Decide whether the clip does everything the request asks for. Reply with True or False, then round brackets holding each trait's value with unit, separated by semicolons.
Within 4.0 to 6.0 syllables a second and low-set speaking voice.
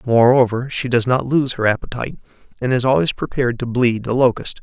True (5.8 syllables/s; 125 Hz)